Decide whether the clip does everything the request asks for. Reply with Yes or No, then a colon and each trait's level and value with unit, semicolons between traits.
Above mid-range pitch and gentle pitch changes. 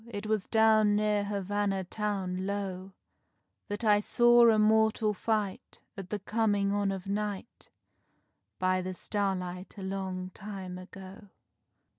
Yes: high, 200 Hz; narrow, 1.9 semitones